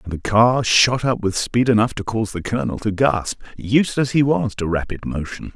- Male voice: Yes, male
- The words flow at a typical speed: No, fast, 225 wpm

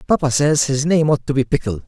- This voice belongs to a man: Yes, male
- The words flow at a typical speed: No, fast, 255 wpm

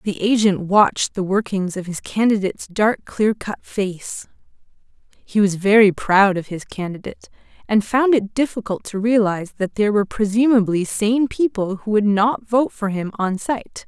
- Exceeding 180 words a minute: No, average, 170 wpm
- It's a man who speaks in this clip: No, female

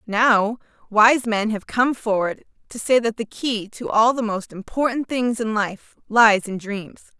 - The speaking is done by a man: No, female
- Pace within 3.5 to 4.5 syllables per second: Yes, 4.0 syllables/s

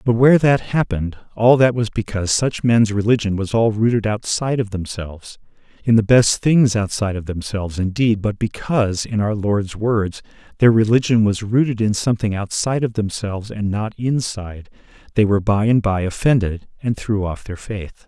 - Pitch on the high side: No, low, 110 Hz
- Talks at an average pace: Yes, average, 180 wpm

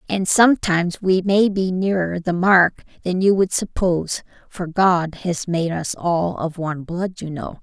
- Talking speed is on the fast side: No, average, 180 wpm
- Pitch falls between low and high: Yes, medium, 180 Hz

